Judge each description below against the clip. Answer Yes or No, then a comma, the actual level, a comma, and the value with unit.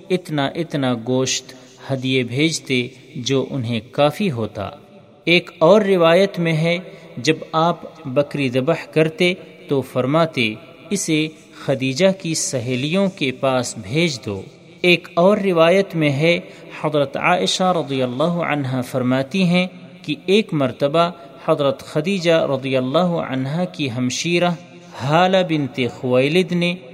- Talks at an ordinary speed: Yes, average, 125 wpm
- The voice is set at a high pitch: No, medium, 155 Hz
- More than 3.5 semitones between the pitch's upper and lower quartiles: Yes, average, 4.7 semitones